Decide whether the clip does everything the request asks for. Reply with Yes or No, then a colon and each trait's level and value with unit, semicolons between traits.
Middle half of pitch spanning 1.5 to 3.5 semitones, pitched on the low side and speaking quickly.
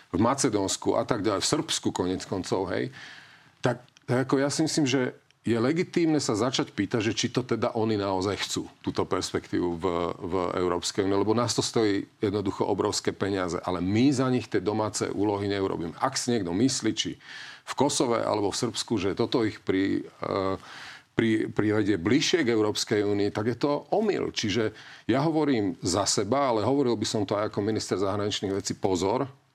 No: average, 4.8 semitones; low, 110 Hz; fast, 185 wpm